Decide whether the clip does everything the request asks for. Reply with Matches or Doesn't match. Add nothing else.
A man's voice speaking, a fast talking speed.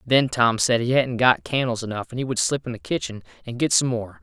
Matches